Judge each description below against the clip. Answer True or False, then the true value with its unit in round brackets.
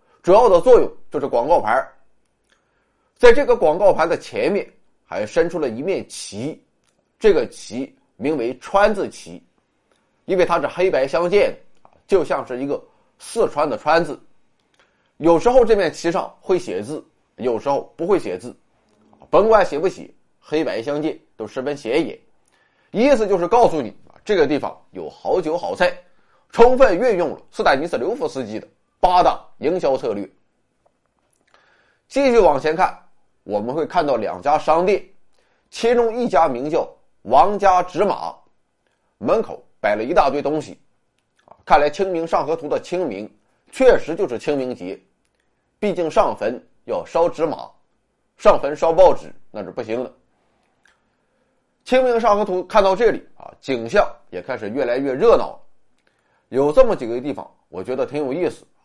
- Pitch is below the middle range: False (215 Hz)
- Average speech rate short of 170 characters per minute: False (225 characters per minute)